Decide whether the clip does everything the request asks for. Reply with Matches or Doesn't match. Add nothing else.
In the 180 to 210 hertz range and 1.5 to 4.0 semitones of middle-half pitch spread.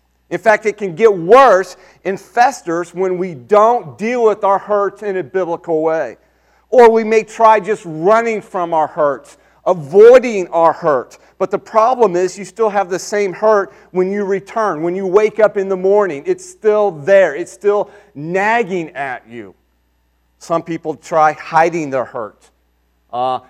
Doesn't match